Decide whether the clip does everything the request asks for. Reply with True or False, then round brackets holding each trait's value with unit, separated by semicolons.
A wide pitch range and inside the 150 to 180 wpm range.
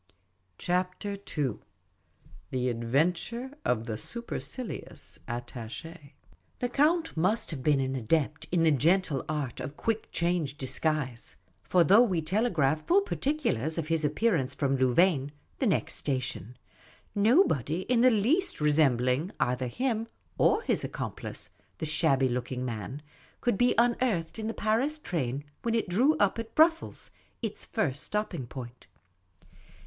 False (9.0 semitones; 140 wpm)